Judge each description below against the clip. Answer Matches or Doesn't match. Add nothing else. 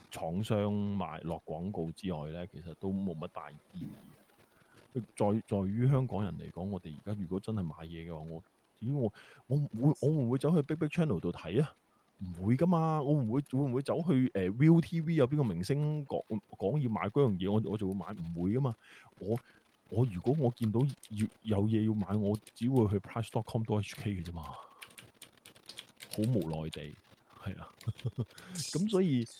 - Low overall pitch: Matches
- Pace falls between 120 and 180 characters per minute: Doesn't match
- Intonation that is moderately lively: Doesn't match